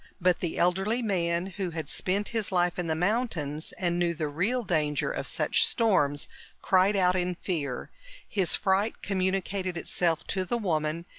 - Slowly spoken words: No, average, 165 wpm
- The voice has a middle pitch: Yes, medium, 180 Hz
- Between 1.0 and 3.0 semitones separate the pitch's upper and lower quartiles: Yes, narrow, 2.6 semitones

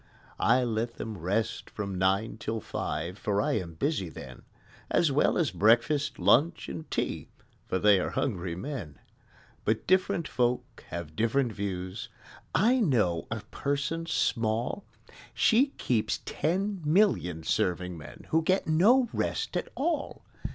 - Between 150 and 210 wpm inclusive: No, average, 140 wpm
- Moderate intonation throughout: No, wide, 9.0 semitones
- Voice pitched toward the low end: Yes, low, 115 Hz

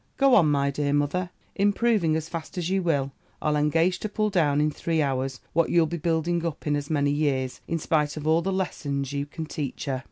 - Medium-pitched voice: Yes, medium, 155 Hz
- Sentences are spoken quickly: Yes, fast, 225 wpm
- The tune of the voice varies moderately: Yes, average, 3.1 semitones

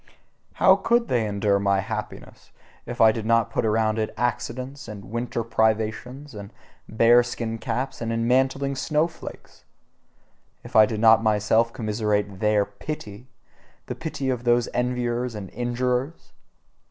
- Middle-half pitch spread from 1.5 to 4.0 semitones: Yes, average, 2.7 semitones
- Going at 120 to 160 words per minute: Yes, average, 140 wpm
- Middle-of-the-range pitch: No, low, 115 Hz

